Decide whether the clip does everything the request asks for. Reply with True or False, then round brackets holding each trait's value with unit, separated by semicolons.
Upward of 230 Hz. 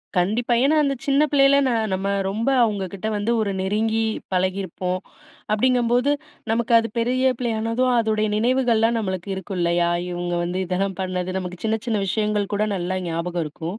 False (210 Hz)